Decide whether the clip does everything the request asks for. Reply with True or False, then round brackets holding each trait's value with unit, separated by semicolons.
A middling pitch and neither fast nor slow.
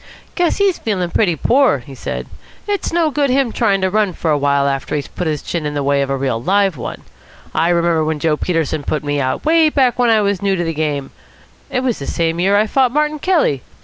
False (175 Hz; 245 wpm)